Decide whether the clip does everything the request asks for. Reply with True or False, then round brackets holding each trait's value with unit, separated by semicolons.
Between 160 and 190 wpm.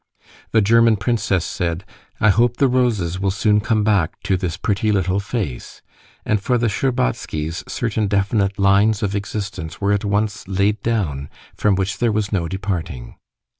True (165 wpm)